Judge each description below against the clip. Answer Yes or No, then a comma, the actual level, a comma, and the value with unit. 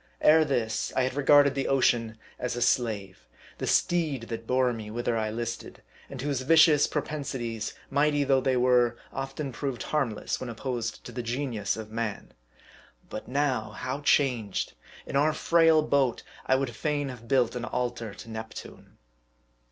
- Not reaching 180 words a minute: Yes, average, 160 wpm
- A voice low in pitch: Yes, low, 125 Hz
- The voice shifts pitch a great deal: No, average, 3.6 semitones